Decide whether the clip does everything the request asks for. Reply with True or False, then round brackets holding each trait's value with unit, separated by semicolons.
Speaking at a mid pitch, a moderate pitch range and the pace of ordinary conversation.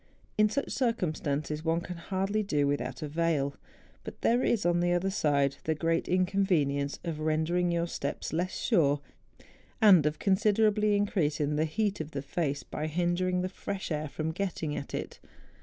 True (170 Hz; 4.2 semitones; 170 wpm)